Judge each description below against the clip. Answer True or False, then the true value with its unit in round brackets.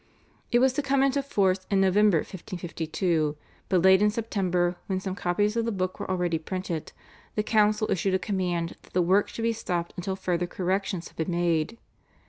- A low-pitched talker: False (190 Hz)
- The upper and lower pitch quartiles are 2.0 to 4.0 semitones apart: True (3.0 semitones)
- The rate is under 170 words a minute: False (190 wpm)